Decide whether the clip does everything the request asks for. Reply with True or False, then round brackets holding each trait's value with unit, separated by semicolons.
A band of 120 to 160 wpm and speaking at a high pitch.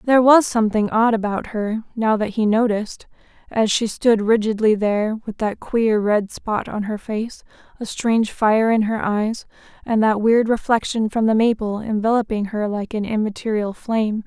False (175 wpm; 220 Hz)